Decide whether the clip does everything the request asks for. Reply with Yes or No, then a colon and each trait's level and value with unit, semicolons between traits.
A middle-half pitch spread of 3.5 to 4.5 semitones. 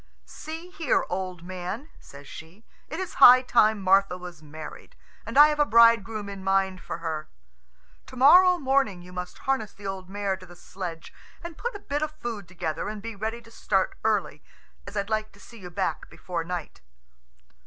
No: average, 5.3 semitones